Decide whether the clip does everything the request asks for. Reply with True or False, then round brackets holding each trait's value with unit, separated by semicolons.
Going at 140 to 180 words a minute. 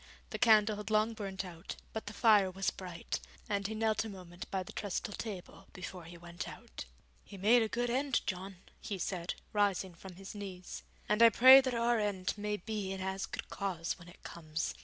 False (205 wpm)